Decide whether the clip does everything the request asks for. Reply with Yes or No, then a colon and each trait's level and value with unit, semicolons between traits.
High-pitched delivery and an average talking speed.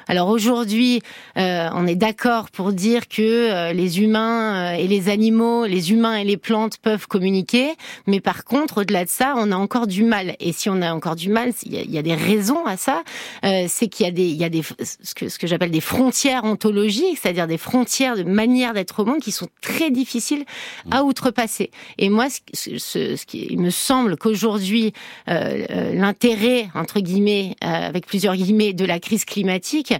Yes: high, 215 Hz; average, 200 wpm